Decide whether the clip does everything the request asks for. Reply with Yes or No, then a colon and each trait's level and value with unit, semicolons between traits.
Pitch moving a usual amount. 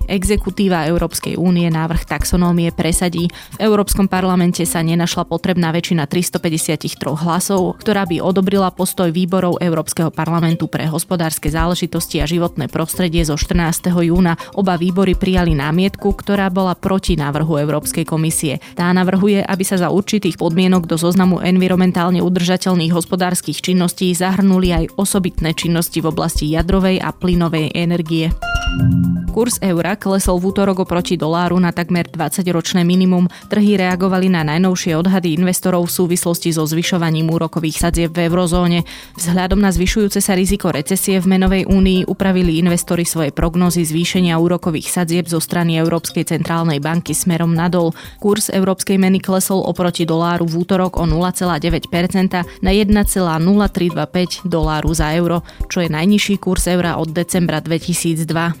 No: narrow, 2.0 semitones